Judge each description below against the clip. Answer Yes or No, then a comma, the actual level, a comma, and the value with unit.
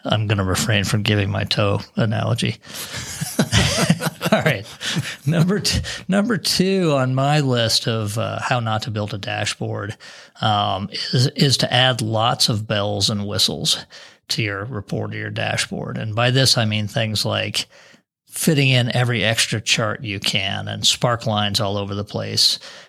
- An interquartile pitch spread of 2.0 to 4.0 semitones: Yes, average, 3.4 semitones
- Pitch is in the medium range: No, low, 110 Hz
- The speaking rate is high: No, average, 165 wpm